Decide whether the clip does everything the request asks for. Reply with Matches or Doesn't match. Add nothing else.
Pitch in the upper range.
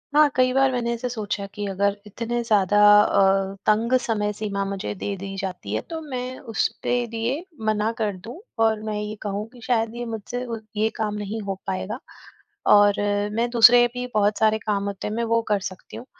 Matches